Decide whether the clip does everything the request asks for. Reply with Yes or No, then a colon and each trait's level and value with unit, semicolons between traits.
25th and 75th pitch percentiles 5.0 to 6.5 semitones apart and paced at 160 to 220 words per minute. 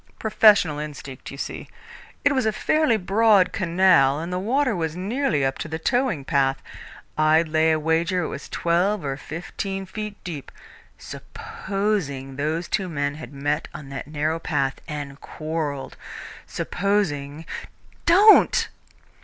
No: wide, 5.6 semitones; average, 145 wpm